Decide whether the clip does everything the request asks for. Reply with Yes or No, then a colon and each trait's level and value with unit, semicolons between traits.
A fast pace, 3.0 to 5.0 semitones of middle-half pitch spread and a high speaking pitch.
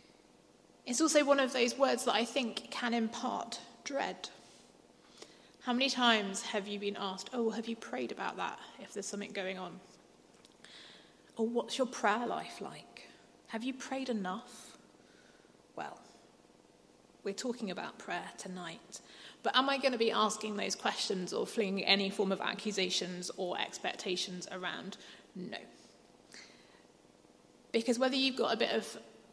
No: average, 145 wpm; average, 3.9 semitones; high, 225 Hz